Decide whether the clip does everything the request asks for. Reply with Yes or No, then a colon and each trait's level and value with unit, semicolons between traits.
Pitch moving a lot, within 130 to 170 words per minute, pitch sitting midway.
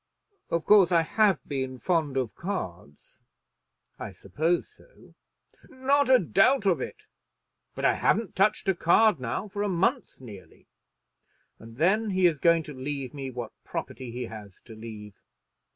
Yes: wide, 8.0 semitones; average, 155 wpm; medium, 160 Hz